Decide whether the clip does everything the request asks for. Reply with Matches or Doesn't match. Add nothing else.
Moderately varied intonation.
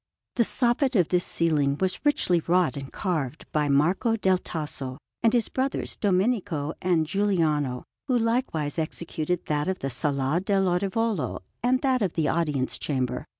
Doesn't match